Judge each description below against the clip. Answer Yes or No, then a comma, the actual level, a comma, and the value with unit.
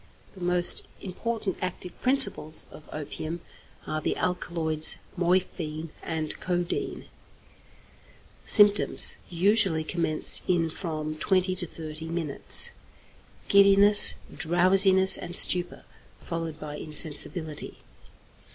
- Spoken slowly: Yes, slow, 95 wpm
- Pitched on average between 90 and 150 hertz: No, medium, 175 Hz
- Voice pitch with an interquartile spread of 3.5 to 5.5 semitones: No, average, 3.0 semitones